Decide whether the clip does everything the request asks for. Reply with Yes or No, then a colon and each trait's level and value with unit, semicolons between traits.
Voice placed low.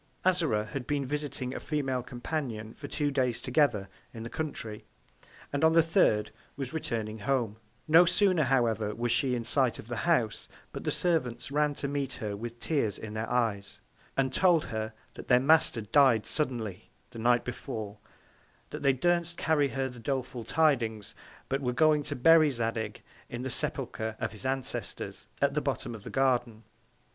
Yes: low, 130 Hz